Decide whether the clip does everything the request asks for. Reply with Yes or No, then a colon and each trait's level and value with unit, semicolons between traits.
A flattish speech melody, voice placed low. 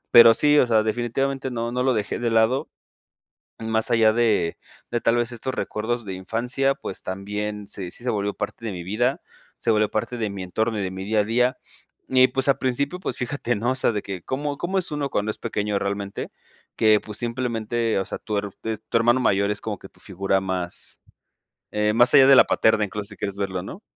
No: average, 3.2 semitones; low, 110 Hz